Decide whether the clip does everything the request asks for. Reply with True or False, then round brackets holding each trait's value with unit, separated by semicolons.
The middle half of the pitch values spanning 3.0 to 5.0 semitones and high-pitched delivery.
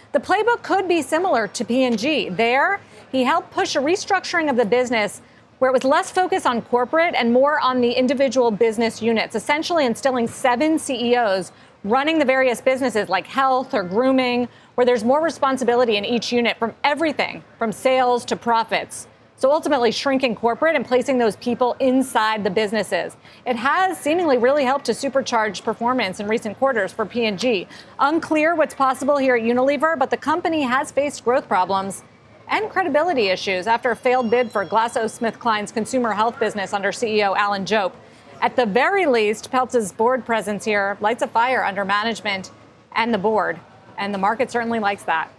True (3.7 semitones; 245 Hz)